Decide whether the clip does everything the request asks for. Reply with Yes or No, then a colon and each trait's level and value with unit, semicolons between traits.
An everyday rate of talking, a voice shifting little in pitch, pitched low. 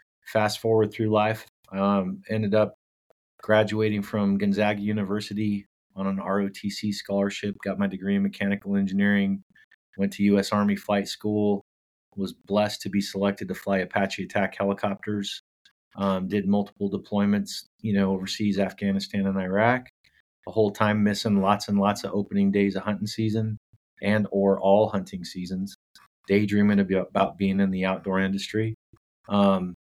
Yes: average, 145 wpm; narrow, 1.1 semitones; low, 100 Hz